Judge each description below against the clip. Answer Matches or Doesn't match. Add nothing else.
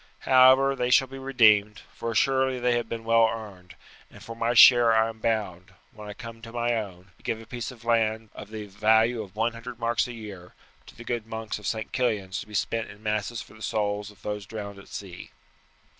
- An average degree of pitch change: Doesn't match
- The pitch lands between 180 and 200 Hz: Doesn't match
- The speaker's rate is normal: Doesn't match